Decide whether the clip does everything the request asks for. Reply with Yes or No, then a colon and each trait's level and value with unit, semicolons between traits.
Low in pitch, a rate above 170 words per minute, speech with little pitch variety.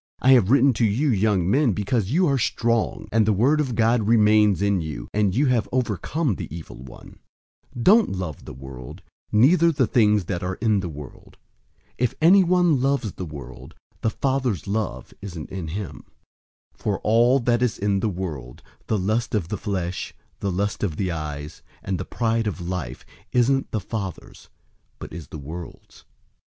No: low, 105 Hz; average, 180 wpm; average, 5.2 semitones